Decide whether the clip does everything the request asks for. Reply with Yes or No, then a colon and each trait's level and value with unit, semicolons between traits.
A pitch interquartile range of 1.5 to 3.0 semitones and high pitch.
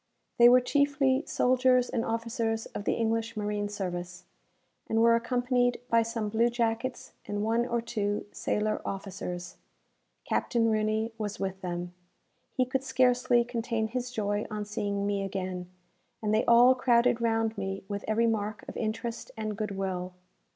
Yes: narrow, 2.6 semitones; high, 225 Hz